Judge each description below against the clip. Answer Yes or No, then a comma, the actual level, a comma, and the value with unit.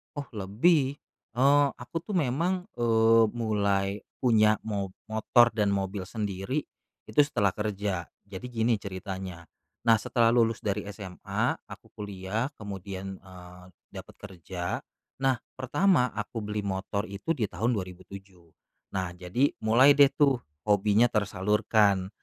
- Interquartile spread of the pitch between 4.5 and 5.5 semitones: No, average, 3.8 semitones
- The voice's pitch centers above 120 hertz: No, low, 105 Hz